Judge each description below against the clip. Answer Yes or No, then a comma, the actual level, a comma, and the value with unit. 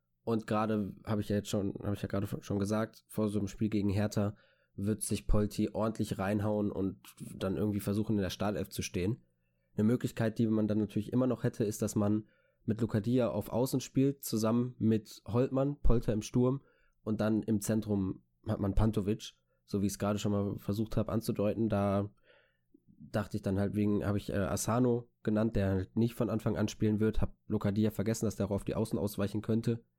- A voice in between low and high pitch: No, low, 105 Hz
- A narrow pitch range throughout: Yes, narrow, 1.7 semitones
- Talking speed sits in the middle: No, fast, 200 wpm